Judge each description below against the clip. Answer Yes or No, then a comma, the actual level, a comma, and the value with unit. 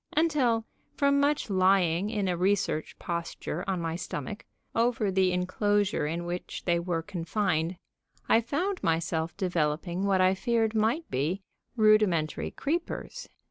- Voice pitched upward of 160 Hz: Yes, high, 190 Hz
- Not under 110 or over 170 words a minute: Yes, slow, 135 wpm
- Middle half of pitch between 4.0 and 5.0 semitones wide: Yes, average, 4.6 semitones